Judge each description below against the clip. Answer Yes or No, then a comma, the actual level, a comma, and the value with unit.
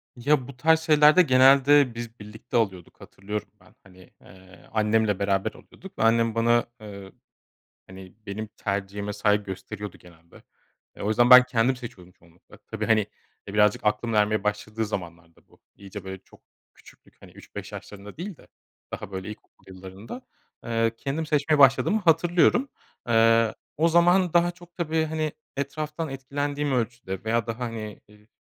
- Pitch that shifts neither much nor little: No, wide, 5.8 semitones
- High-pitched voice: No, low, 115 Hz